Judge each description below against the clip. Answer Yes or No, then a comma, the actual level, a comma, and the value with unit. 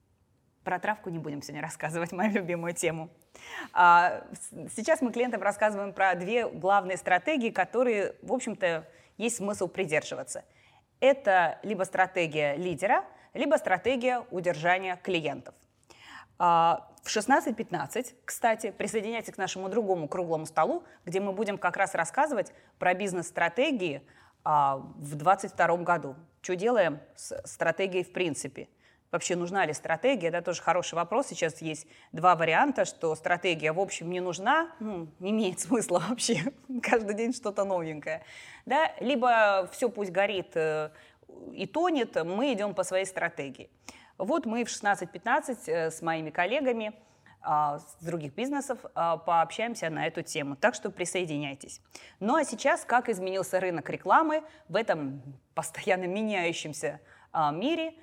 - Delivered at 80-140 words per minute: Yes, average, 130 wpm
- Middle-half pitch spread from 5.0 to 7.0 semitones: Yes, wide, 5.6 semitones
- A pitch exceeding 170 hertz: Yes, medium, 185 Hz